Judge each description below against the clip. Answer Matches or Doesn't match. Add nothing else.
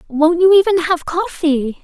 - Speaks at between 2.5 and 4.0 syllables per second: Doesn't match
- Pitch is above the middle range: Matches